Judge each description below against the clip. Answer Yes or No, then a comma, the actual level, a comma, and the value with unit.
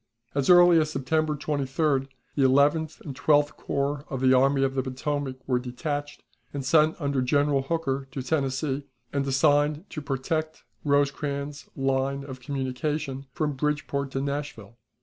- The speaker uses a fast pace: No, average, 150 wpm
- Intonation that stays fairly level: Yes, narrow, 1.8 semitones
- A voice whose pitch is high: No, medium, 140 Hz